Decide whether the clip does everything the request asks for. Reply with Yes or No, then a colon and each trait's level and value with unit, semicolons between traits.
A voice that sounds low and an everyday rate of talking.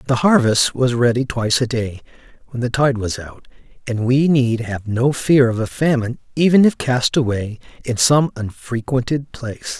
Yes: low, 125 Hz; average, 180 wpm